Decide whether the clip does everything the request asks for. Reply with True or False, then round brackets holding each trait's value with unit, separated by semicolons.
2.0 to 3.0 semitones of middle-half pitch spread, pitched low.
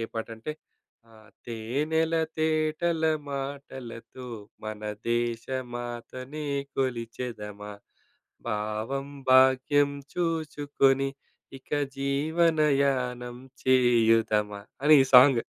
False (3.9 semitones; 130 Hz)